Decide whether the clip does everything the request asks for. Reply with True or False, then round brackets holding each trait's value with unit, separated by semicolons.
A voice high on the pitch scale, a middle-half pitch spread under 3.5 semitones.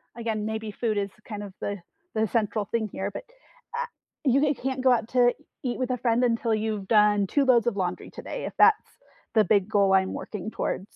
True (220 Hz; 2.9 semitones)